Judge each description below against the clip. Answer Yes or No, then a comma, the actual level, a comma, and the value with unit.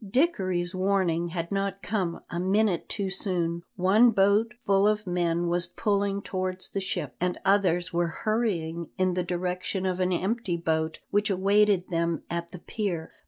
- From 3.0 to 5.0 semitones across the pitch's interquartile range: No, narrow, 2.6 semitones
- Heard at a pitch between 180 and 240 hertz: Yes, medium, 185 Hz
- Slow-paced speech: No, average, 165 wpm